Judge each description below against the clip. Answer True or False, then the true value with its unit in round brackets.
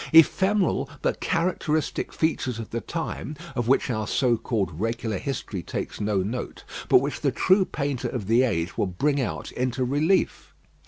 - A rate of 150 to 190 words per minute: True (165 wpm)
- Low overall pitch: True (130 Hz)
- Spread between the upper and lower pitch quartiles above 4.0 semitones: True (5.1 semitones)